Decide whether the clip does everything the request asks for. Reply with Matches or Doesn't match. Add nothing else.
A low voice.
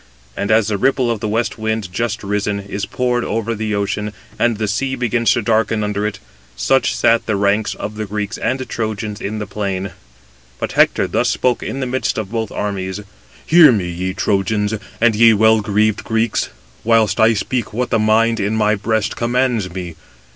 Matches